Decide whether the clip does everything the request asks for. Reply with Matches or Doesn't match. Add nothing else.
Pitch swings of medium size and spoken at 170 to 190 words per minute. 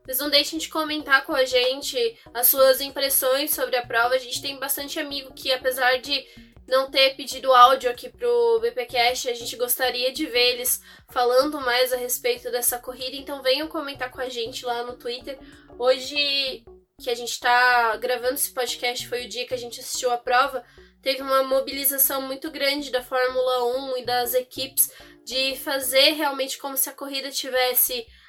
Doesn't match